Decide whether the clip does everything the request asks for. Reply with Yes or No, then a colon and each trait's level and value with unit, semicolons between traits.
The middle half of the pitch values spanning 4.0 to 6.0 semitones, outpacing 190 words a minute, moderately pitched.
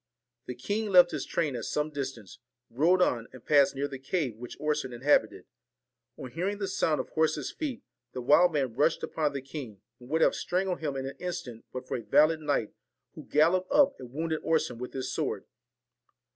Yes: average, 4.5 semitones; average, 200 wpm; medium, 150 Hz